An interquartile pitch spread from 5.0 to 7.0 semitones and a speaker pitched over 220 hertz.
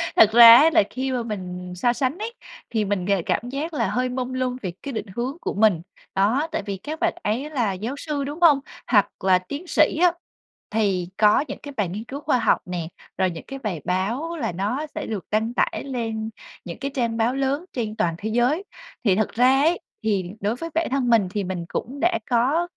Yes: wide, 5.4 semitones; high, 235 Hz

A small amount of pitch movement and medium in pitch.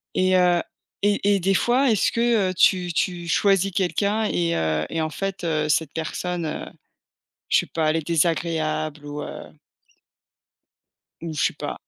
No: average, 3.7 semitones; medium, 175 Hz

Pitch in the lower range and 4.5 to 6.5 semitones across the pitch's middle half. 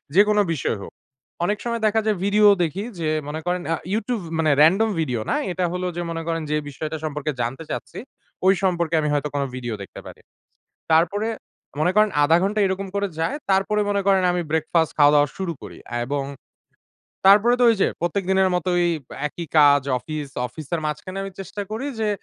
No: medium, 175 Hz; average, 4.8 semitones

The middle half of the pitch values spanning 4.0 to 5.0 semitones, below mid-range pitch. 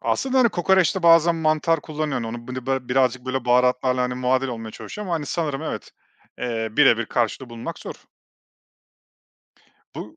Yes: average, 4.5 semitones; low, 130 Hz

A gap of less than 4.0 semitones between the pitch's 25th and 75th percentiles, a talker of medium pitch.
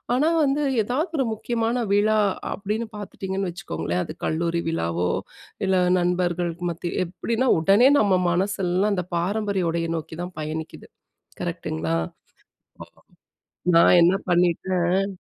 Yes: average, 3.4 semitones; medium, 180 Hz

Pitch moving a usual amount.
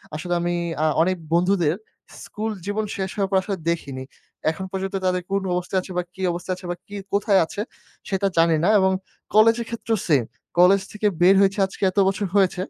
No: narrow, 2.2 semitones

